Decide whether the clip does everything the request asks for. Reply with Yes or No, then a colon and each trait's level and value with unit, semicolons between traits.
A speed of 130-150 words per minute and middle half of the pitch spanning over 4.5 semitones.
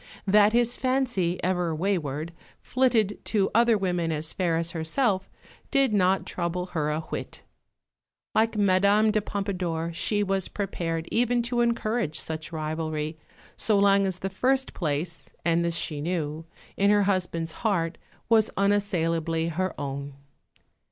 No: average, 140 wpm; average, 4.2 semitones